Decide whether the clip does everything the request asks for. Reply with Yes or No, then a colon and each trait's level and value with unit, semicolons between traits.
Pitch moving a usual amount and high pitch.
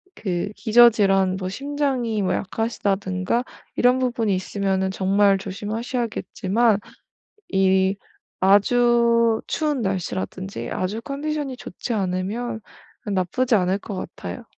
Yes: average, 4.0 semitones; high, 205 Hz